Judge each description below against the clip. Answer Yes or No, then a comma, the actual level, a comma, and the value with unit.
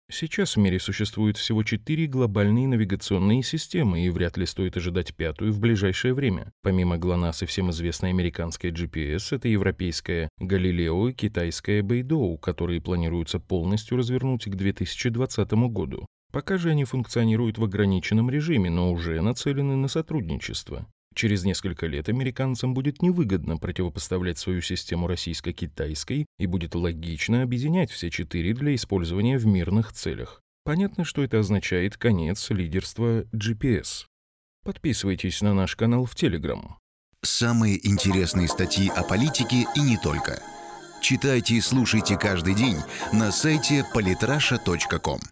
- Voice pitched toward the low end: Yes, low, 100 Hz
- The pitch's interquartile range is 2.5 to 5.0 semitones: No, wide, 5.4 semitones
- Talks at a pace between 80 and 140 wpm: Yes, average, 130 wpm